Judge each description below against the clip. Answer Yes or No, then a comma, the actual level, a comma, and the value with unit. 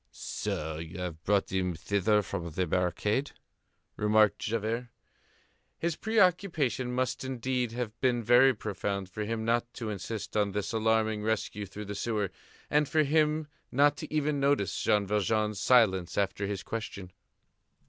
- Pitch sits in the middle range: No, low, 110 Hz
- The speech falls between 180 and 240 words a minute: No, average, 150 wpm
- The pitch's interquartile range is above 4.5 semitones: No, average, 4.2 semitones